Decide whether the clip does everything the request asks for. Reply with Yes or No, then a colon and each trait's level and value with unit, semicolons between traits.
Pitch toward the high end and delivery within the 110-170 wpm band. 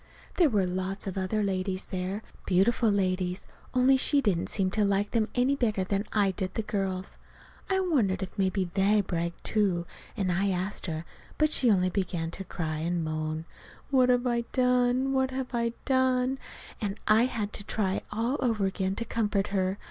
No: high, 200 Hz; average, 185 wpm